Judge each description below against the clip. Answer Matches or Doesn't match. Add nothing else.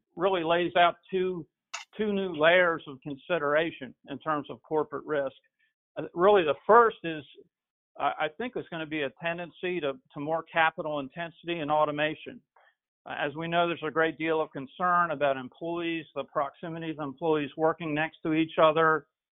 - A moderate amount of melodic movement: Doesn't match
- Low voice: Doesn't match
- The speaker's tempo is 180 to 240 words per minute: Doesn't match